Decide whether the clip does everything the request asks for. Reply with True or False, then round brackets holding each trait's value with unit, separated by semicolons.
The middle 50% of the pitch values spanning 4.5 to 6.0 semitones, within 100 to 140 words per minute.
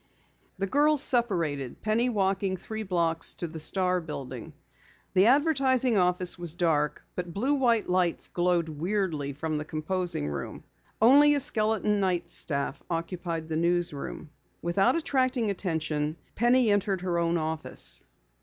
True (5.2 semitones; 135 wpm)